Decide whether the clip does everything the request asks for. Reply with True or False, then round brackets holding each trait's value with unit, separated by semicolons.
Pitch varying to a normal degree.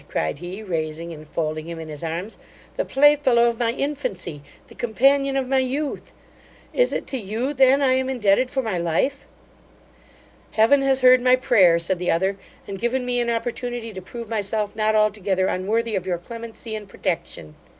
False (5.8 semitones)